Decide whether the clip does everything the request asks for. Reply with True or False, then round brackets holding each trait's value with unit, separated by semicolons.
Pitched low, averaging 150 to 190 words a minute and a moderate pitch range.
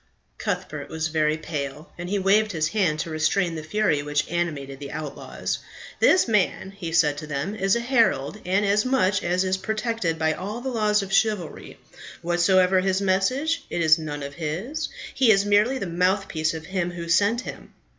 False (185 Hz; 185 wpm; 4.7 semitones)